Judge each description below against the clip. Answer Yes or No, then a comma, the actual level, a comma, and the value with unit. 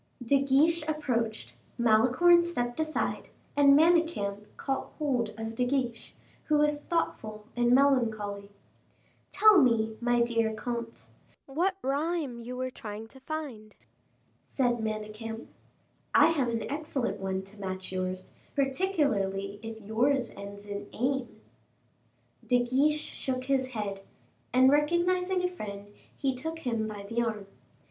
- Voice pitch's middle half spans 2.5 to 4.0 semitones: No, average, 5.1 semitones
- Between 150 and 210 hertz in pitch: No, high, 245 Hz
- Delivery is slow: Yes, slow, 130 wpm